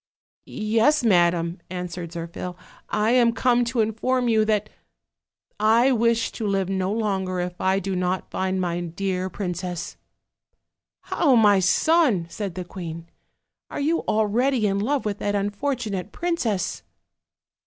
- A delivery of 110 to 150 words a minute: Yes, average, 140 wpm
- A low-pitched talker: No, high, 205 Hz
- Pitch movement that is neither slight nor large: Yes, average, 4.2 semitones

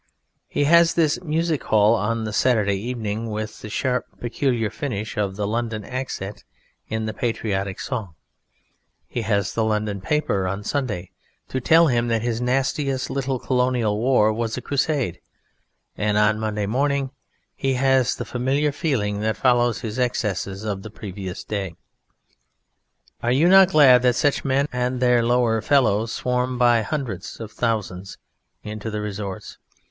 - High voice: No, low, 115 Hz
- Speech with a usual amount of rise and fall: Yes, average, 3.8 semitones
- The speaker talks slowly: No, average, 155 wpm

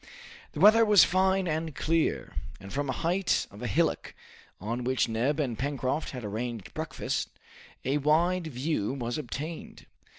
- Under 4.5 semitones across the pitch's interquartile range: No, average, 5.2 semitones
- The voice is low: No, medium, 145 Hz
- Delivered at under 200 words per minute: Yes, average, 155 wpm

